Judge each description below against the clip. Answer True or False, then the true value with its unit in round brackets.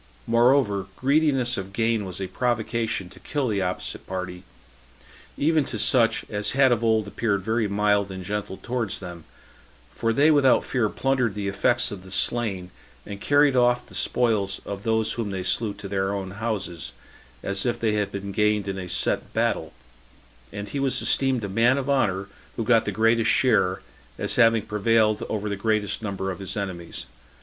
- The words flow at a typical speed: True (180 wpm)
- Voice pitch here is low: True (105 Hz)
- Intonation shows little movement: False (3.4 semitones)